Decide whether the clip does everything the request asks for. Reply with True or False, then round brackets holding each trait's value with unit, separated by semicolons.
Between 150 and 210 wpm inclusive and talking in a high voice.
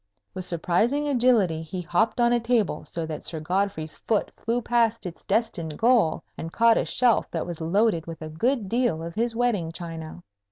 True (190 wpm; 195 Hz)